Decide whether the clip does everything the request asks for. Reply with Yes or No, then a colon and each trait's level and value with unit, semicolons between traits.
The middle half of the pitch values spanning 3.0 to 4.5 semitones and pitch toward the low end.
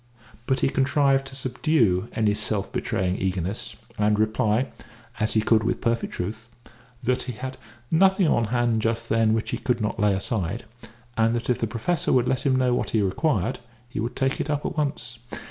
Yes: average, 3.5 semitones; low, 115 Hz